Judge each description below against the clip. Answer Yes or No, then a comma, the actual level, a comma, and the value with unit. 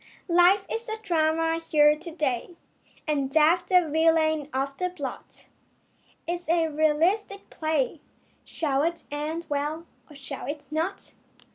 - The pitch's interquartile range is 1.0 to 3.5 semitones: Yes, narrow, 2.6 semitones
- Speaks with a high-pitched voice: Yes, very high, 315 Hz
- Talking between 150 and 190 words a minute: No, average, 140 wpm